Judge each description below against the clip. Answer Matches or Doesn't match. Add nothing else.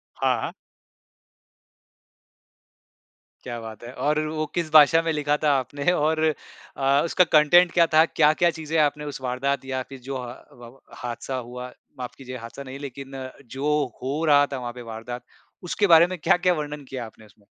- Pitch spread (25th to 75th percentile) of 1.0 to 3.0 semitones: Doesn't match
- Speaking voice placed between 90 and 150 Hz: Matches